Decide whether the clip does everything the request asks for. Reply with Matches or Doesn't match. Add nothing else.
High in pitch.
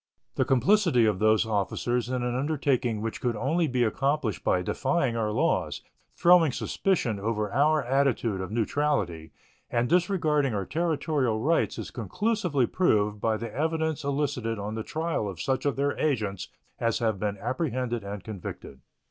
Doesn't match